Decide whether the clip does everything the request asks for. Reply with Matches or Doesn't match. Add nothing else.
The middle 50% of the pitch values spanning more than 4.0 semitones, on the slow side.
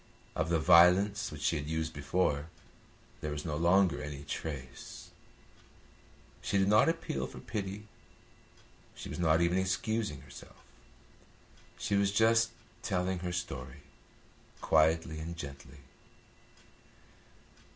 Matches